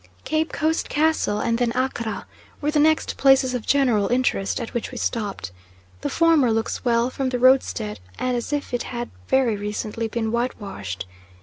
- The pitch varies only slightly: No, average, 3.2 semitones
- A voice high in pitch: Yes, high, 245 Hz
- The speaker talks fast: No, average, 180 wpm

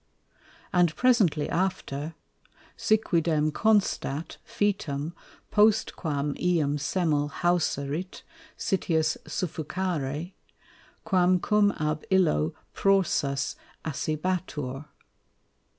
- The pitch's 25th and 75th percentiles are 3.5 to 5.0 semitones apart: Yes, average, 4.2 semitones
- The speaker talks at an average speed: No, slow, 70 wpm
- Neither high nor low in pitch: Yes, medium, 165 Hz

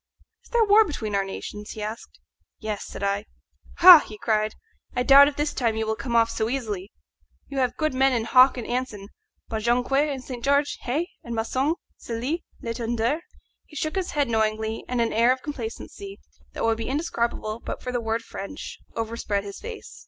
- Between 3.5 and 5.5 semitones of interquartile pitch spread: Yes, average, 4.1 semitones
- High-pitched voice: Yes, high, 235 Hz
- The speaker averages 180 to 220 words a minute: Yes, average, 195 wpm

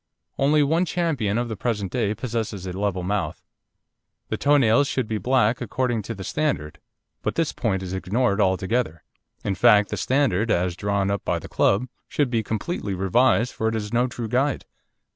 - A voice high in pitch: No, low, 110 Hz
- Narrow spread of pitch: No, average, 4.3 semitones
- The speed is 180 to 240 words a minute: Yes, average, 185 wpm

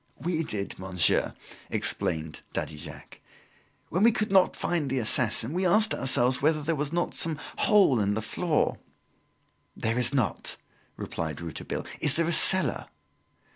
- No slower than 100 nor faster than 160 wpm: Yes, average, 155 wpm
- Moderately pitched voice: Yes, medium, 145 Hz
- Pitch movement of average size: No, wide, 8.0 semitones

